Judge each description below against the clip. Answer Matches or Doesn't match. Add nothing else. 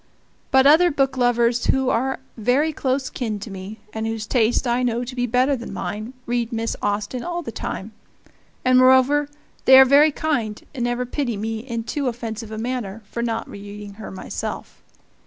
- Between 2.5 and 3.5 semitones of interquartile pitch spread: Matches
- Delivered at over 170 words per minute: Matches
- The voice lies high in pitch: Matches